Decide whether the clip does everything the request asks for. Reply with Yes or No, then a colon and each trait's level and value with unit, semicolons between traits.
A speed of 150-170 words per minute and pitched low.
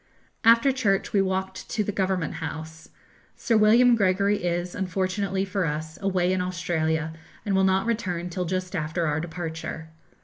No: average, 160 wpm; medium, 185 Hz